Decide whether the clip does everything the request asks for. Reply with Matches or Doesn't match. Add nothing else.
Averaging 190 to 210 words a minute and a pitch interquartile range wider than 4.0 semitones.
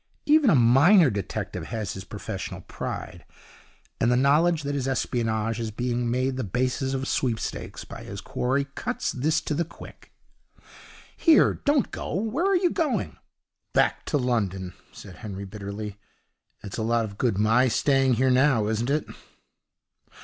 Doesn't match